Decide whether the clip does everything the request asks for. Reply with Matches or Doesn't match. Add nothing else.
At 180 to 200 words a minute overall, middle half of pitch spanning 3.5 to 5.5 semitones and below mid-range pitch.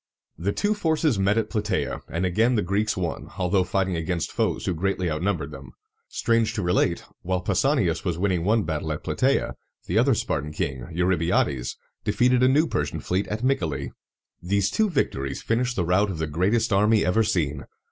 Matches